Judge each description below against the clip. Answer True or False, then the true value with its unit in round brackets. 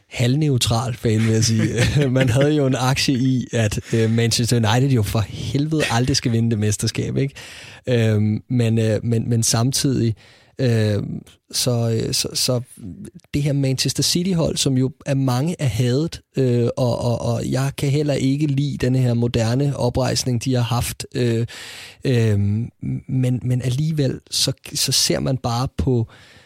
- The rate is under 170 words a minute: True (145 wpm)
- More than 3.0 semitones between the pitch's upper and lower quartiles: False (2.7 semitones)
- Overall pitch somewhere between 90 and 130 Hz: True (125 Hz)